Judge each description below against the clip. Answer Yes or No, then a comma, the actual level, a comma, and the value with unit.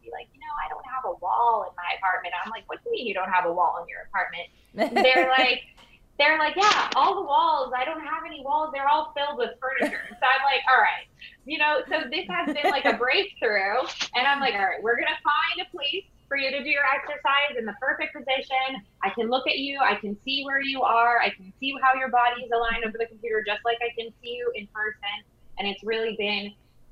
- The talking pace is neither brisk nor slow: No, fast, 250 wpm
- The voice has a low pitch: No, very high, 265 Hz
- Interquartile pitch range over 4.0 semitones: Yes, average, 4.7 semitones